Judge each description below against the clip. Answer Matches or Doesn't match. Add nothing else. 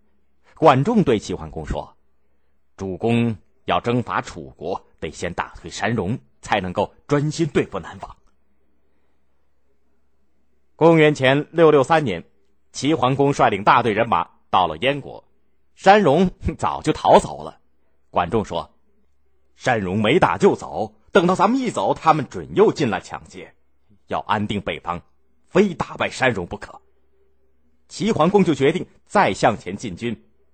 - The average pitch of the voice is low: Matches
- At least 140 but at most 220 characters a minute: Matches